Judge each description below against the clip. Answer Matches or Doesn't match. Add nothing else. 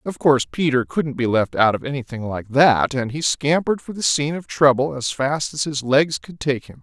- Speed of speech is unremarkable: Doesn't match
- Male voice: Matches